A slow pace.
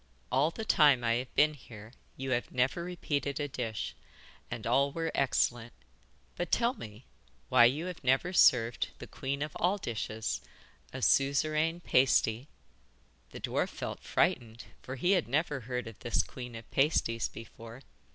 No: average, 160 wpm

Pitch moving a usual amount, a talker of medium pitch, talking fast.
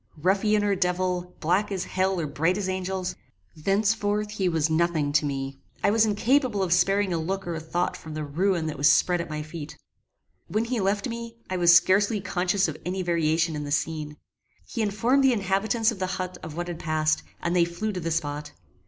Yes: average, 4.1 semitones; medium, 180 Hz; fast, 210 wpm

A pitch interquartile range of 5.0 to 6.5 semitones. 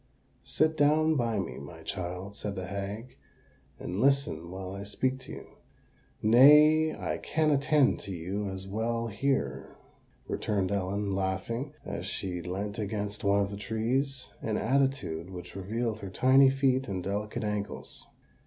Yes: wide, 5.4 semitones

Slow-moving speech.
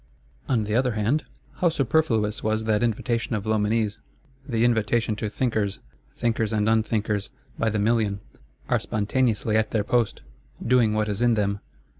No: average, 155 wpm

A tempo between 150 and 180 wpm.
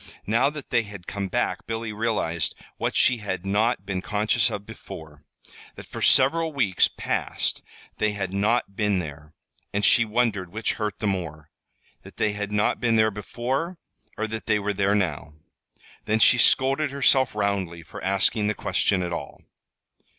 Yes: average, 170 wpm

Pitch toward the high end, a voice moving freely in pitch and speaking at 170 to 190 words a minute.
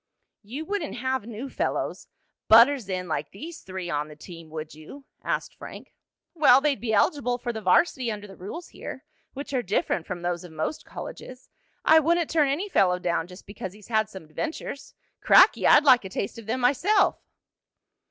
Yes: high, 225 Hz; wide, 7.6 semitones; average, 185 wpm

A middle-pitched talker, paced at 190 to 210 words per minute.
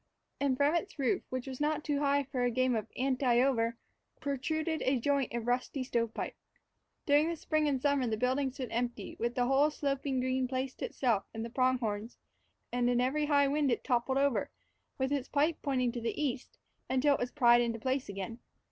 No: very high, 260 Hz; average, 200 wpm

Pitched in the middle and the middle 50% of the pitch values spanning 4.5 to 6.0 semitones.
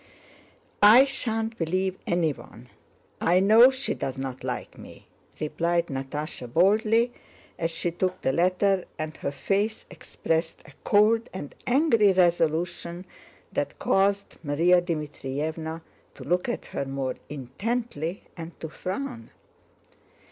Yes: medium, 175 Hz; average, 5.0 semitones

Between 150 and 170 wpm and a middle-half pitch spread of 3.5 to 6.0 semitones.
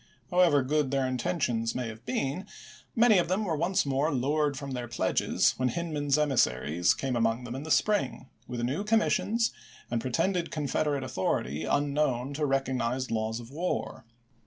Yes: average, 165 wpm; average, 4.2 semitones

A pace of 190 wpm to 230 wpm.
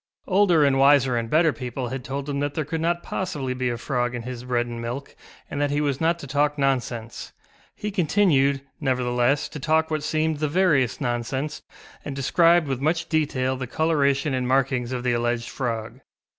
Yes: average, 195 wpm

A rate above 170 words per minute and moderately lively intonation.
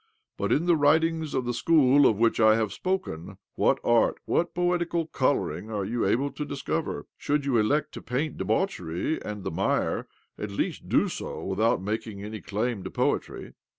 No: average, 185 wpm; wide, 6.4 semitones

